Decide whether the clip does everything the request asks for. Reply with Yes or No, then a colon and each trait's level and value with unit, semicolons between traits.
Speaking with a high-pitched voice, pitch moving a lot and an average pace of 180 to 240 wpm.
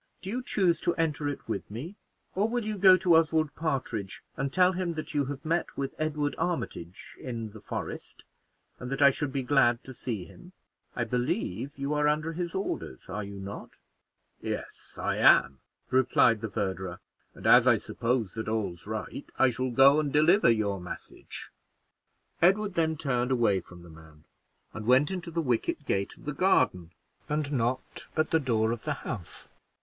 No: low, 135 Hz; wide, 6.5 semitones; average, 185 wpm